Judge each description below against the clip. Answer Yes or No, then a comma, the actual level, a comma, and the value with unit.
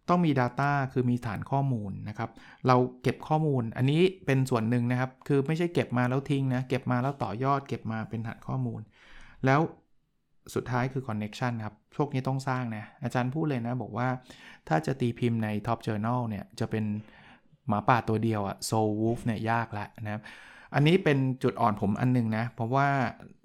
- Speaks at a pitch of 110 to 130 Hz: Yes, low, 125 Hz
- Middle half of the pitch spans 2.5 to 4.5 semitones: Yes, average, 3.1 semitones